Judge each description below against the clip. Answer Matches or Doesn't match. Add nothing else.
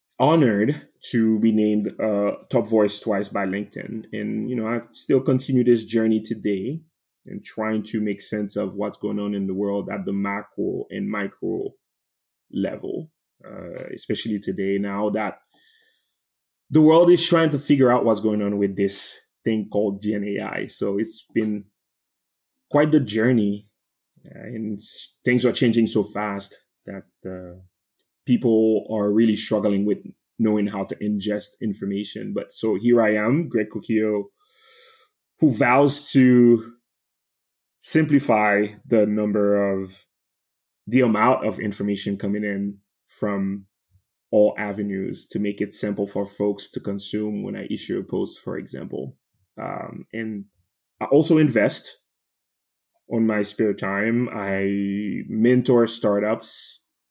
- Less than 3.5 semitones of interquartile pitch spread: Matches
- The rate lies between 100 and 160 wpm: Matches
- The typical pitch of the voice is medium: Doesn't match